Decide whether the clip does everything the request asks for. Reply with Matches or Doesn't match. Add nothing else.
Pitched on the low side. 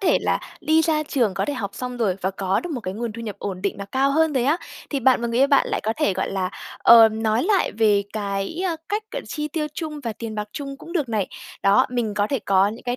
Doesn't match